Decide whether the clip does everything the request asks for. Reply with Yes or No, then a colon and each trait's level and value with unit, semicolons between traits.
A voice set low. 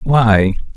Yes: low, 110 Hz